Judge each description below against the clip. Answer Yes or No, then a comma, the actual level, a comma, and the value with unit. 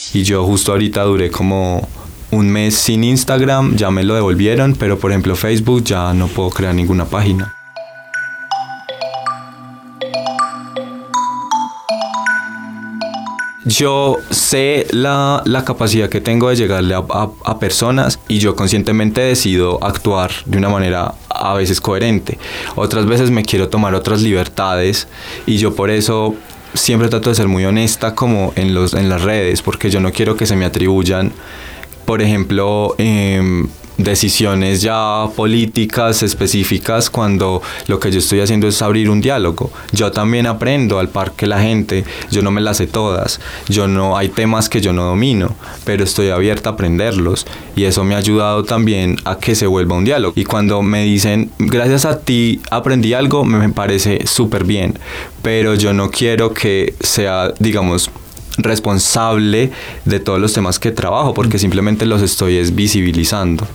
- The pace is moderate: Yes, average, 160 wpm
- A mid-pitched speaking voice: No, low, 105 Hz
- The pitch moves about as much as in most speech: Yes, average, 3.2 semitones